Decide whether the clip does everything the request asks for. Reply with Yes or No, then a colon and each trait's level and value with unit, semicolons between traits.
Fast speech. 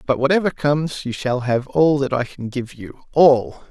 No: average, 195 wpm